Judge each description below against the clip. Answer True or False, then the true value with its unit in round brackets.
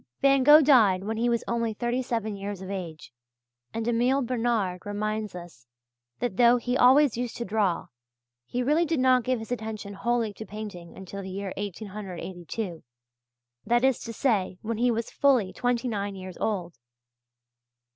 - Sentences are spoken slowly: False (165 wpm)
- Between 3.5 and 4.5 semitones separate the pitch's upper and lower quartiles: True (3.8 semitones)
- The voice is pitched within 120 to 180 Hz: False (220 Hz)